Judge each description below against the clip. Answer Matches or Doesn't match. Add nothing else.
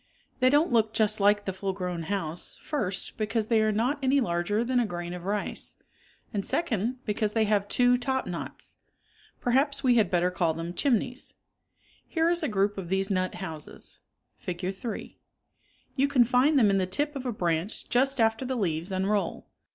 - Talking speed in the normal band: Matches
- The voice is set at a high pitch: Matches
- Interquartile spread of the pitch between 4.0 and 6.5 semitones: Matches